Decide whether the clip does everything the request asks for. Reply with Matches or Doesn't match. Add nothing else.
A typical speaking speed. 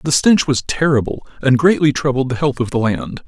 Doesn't match